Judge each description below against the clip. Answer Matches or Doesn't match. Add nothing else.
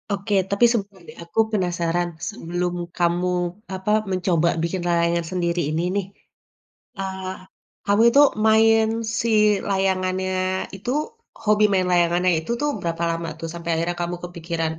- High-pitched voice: Doesn't match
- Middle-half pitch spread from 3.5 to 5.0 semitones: Doesn't match